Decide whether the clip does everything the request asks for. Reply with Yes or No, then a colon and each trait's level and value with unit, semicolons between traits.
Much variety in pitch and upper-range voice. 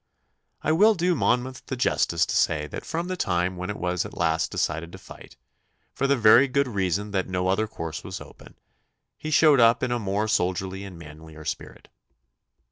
No: wide, 6.5 semitones; low, 100 Hz